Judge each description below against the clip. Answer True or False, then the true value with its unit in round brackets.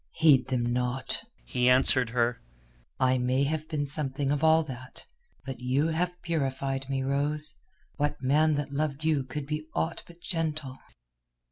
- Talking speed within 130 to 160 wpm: True (155 wpm)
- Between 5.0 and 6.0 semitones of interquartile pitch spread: False (3.0 semitones)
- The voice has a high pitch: False (140 Hz)